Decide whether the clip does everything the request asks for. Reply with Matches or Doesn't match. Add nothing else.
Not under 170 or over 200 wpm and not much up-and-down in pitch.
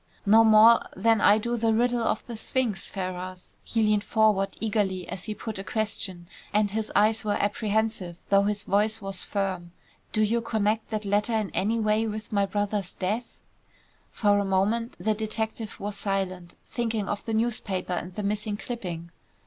Matches